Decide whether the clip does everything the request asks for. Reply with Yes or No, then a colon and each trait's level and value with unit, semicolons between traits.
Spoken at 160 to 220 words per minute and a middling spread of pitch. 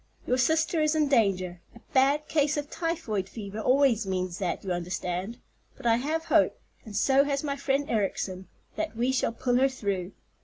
No: average, 180 wpm; wide, 6.4 semitones